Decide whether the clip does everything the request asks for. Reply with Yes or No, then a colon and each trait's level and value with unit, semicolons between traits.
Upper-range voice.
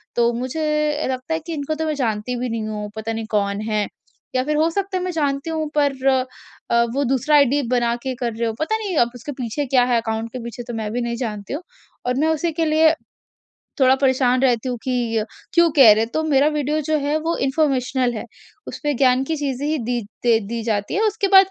Yes: very high, 260 Hz